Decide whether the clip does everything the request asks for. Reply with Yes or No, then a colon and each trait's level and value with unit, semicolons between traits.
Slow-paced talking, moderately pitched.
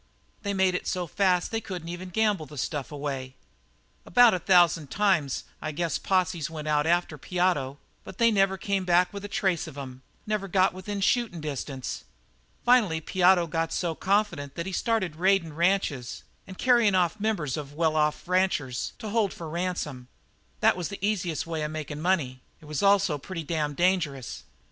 No: average, 180 wpm; medium, 175 Hz